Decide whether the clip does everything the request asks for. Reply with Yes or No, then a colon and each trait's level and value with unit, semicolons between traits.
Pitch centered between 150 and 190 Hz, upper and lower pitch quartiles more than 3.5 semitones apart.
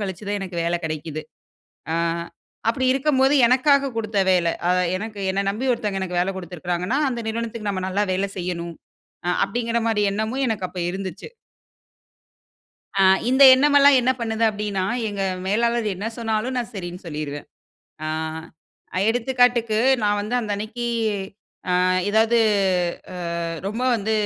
No: high, 215 Hz; average, 4.0 semitones